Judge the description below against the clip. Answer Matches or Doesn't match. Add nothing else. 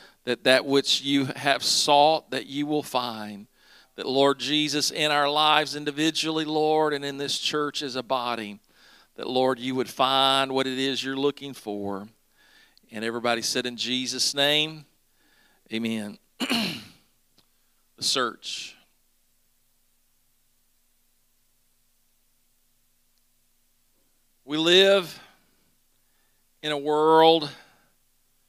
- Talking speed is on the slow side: Matches